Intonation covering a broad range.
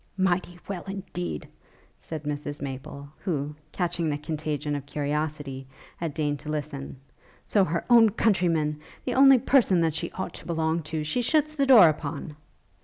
No: average, 4.3 semitones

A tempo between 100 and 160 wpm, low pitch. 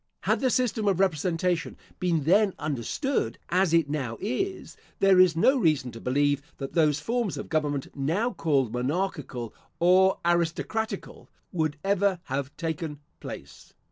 No: average, 140 wpm; medium, 165 Hz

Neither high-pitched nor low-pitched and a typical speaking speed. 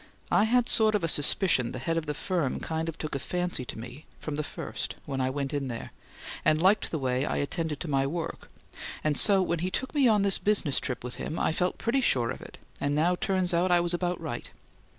No: medium, 160 Hz; fast, 250 wpm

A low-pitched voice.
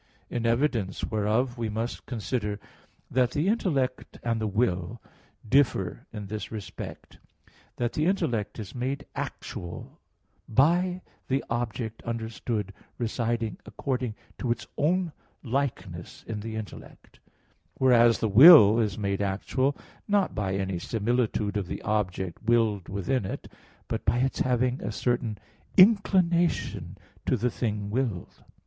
Yes: low, 115 Hz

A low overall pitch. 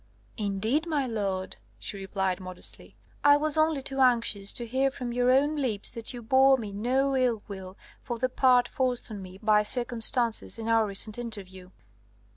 No: high, 235 Hz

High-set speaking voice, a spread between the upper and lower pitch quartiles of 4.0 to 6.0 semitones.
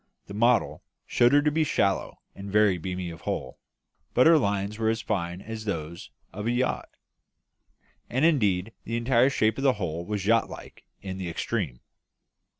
No: low, 105 Hz; average, 4.4 semitones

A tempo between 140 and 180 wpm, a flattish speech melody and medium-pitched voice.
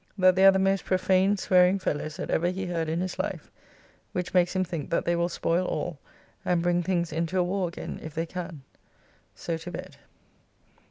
No: fast, 205 wpm; narrow, 1.8 semitones; medium, 180 Hz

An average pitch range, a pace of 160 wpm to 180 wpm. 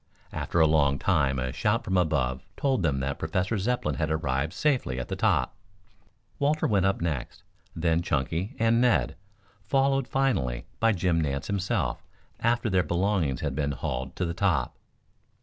No: wide, 7.2 semitones; average, 165 wpm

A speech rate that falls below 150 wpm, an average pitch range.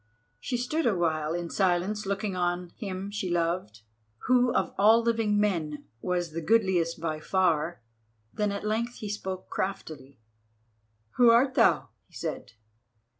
Yes: average, 140 wpm; average, 4.1 semitones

